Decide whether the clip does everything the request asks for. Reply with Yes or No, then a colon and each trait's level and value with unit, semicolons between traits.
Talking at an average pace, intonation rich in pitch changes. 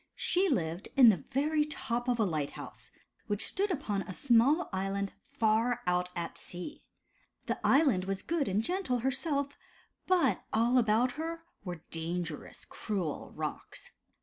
Yes: average, 150 wpm; wide, 7.2 semitones